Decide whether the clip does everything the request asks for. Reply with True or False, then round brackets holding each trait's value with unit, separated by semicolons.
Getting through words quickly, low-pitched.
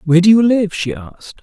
False (255 wpm; 185 Hz)